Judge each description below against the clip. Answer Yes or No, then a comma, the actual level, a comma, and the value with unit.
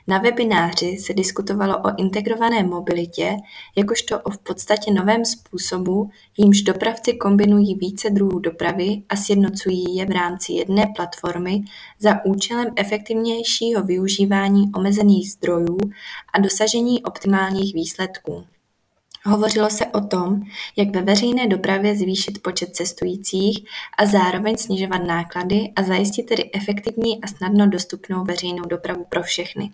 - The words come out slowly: No, average, 125 wpm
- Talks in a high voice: Yes, high, 200 Hz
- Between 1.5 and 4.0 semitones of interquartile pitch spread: Yes, narrow, 2.6 semitones